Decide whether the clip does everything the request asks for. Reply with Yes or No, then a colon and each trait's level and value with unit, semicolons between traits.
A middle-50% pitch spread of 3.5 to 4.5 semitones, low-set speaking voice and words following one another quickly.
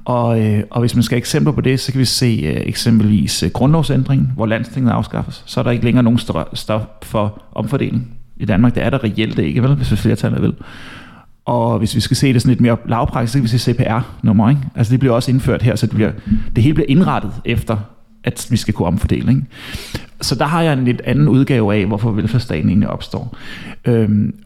No: average, 2.7 semitones; low, 120 Hz; fast, 230 wpm